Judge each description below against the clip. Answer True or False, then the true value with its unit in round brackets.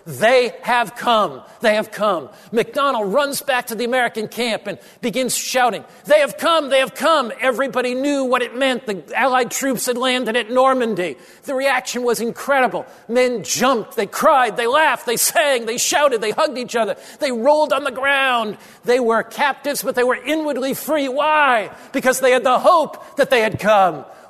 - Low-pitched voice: False (250 Hz)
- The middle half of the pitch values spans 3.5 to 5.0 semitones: False (2.9 semitones)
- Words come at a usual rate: True (185 wpm)